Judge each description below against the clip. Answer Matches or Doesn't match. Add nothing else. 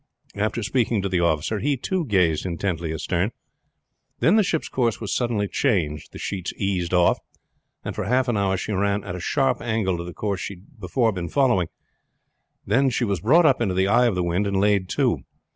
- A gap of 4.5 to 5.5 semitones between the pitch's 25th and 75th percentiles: Matches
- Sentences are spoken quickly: Matches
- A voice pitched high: Doesn't match